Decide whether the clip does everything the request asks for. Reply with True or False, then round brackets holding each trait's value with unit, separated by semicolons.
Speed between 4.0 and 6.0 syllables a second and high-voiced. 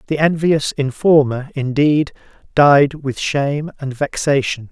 False (4.1 syllables/s; 140 Hz)